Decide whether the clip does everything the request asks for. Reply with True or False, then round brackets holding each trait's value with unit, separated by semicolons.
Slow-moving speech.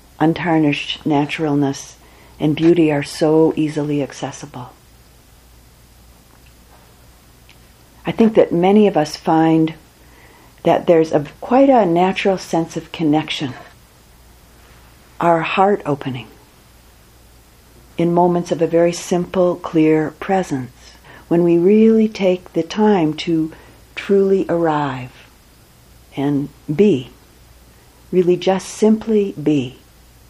True (100 wpm)